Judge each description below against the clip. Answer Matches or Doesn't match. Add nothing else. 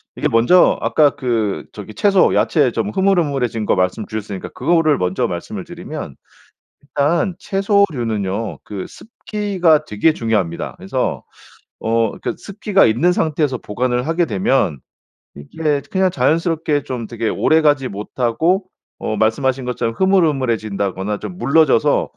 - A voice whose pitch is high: Doesn't match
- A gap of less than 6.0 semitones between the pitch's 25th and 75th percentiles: Doesn't match